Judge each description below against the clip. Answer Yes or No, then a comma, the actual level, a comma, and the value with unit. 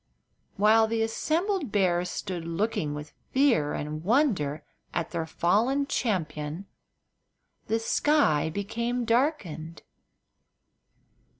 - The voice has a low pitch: No, high, 205 Hz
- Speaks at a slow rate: Yes, slow, 95 wpm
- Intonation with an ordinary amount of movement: No, wide, 6.9 semitones